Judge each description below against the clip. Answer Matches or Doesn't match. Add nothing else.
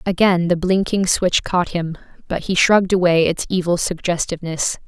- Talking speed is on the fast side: Doesn't match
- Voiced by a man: Doesn't match